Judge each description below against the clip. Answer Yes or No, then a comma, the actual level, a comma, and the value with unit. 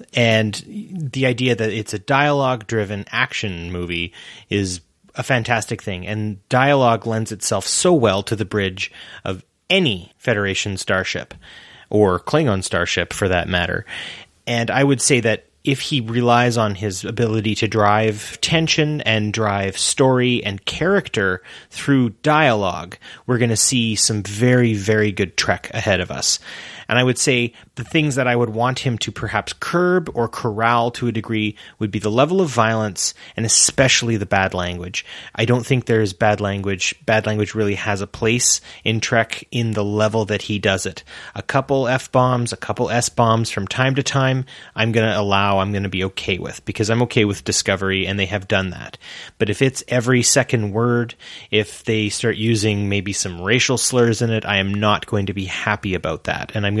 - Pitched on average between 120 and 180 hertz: No, low, 110 Hz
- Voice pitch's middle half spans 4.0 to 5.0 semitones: No, average, 3.4 semitones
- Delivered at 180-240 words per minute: Yes, average, 185 wpm